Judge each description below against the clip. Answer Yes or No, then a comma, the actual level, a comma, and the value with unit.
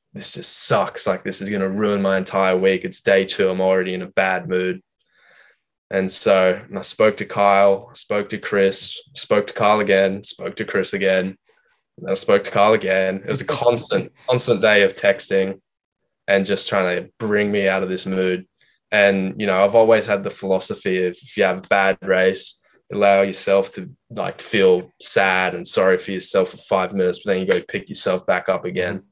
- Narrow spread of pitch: Yes, narrow, 1.6 semitones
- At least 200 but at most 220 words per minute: Yes, fast, 205 wpm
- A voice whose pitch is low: Yes, very low, 95 Hz